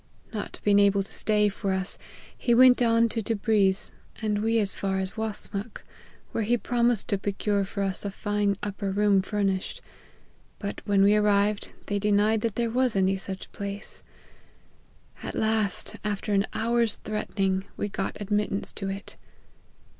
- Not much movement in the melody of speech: Yes, narrow, 1.7 semitones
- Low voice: No, high, 205 Hz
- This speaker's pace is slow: No, average, 160 wpm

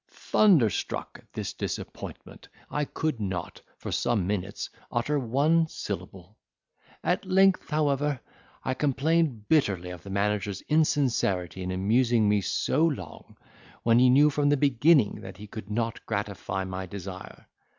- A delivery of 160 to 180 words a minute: No, average, 140 wpm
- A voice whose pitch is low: Yes, low, 115 Hz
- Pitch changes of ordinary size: No, wide, 7.1 semitones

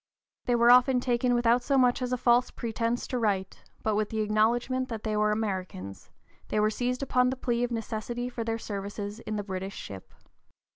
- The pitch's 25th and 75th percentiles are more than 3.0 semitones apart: No, narrow, 2.6 semitones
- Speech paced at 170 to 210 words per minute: Yes, fast, 205 wpm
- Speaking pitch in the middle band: No, high, 230 Hz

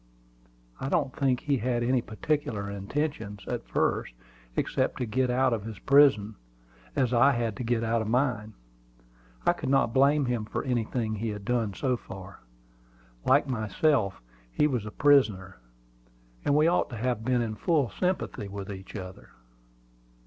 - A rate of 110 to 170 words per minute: Yes, average, 165 wpm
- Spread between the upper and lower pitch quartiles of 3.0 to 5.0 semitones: Yes, average, 4.2 semitones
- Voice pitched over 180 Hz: No, low, 120 Hz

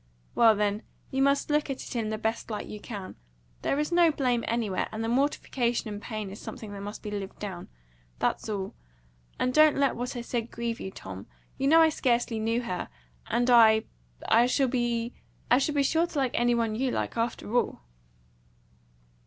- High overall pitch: Yes, high, 235 Hz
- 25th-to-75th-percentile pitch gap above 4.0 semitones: No, average, 3.6 semitones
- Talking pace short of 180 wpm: No, average, 190 wpm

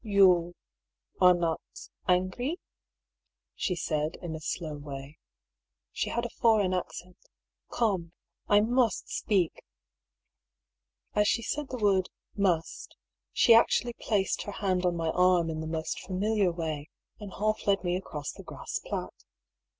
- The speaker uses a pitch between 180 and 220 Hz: Yes, medium, 185 Hz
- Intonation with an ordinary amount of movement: Yes, average, 3.8 semitones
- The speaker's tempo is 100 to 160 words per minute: Yes, average, 150 wpm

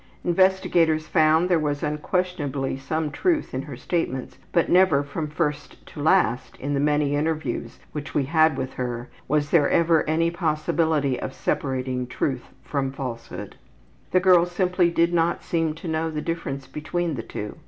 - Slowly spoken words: No, average, 165 wpm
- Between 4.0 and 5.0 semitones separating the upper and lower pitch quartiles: No, average, 3.3 semitones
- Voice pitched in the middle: Yes, medium, 155 Hz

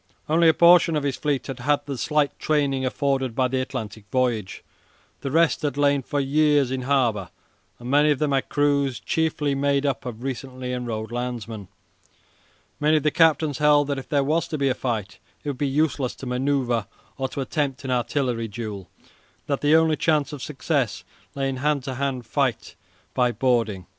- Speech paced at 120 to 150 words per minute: No, average, 195 wpm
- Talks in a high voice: No, low, 135 Hz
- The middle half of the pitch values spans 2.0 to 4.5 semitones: Yes, average, 2.8 semitones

